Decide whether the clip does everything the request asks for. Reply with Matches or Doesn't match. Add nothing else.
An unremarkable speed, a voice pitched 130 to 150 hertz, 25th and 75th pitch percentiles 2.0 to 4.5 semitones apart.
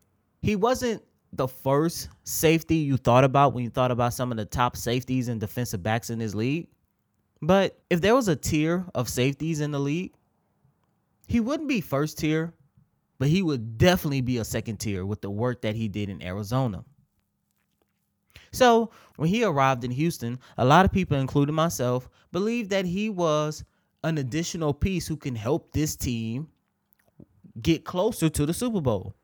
Doesn't match